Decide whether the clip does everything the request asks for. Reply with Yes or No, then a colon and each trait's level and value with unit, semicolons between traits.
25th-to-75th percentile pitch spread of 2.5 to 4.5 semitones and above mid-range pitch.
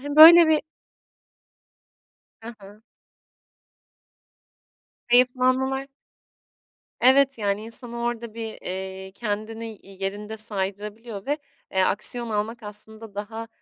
Yes: average, 3.1 semitones; high, 225 Hz